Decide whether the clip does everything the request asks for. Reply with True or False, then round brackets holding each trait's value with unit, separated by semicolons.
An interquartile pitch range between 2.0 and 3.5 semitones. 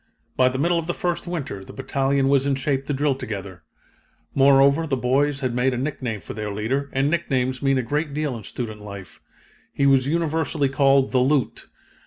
True (2.4 semitones)